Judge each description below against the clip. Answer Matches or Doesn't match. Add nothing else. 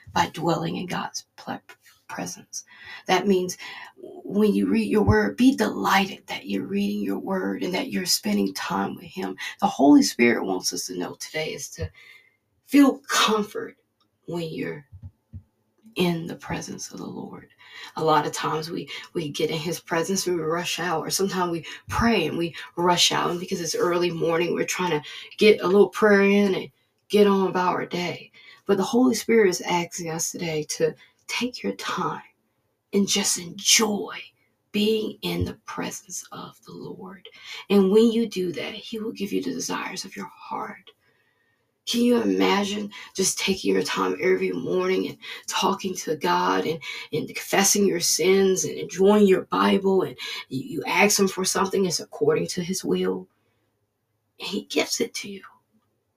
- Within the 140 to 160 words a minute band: Doesn't match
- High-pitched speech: Doesn't match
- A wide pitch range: Matches